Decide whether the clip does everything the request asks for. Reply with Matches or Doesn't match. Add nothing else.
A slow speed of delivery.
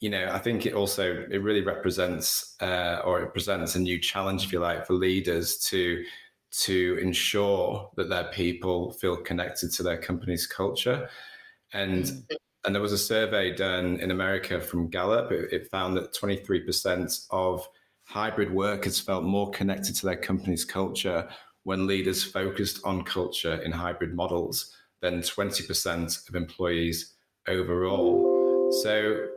Doesn't match